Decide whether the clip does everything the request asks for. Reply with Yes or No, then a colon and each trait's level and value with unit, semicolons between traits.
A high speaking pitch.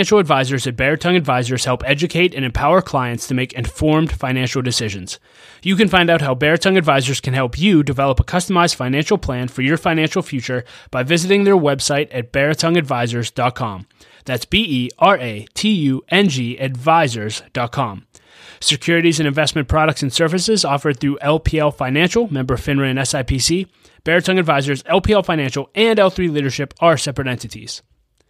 No: medium, 140 Hz